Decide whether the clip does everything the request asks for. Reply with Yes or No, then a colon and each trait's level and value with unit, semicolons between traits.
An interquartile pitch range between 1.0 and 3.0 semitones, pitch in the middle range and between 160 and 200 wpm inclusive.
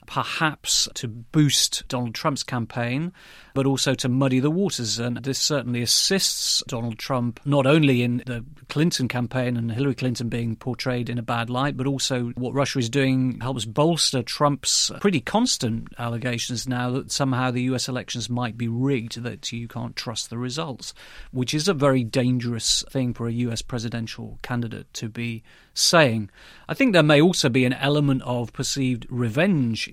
No: narrow, 2.6 semitones; low, 125 Hz; average, 170 wpm